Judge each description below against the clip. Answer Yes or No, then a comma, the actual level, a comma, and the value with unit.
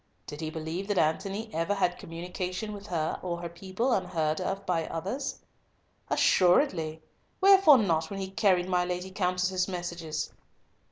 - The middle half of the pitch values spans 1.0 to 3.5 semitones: Yes, average, 2.9 semitones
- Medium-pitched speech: Yes, medium, 180 Hz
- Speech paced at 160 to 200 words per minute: No, average, 145 wpm